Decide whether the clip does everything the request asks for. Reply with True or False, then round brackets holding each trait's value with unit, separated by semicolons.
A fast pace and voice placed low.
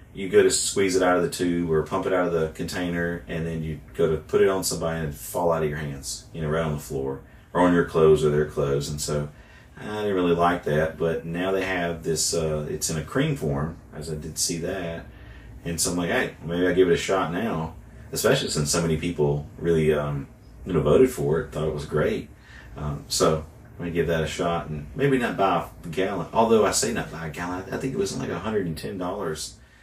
True (255 wpm; 80 Hz)